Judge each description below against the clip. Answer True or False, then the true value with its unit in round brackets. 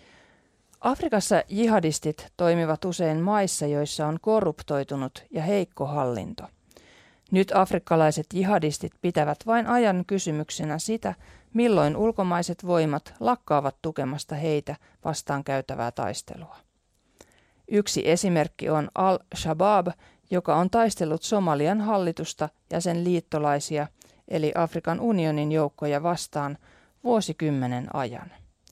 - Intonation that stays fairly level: False (4.5 semitones)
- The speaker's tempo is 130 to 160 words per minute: False (100 wpm)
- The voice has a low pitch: False (165 Hz)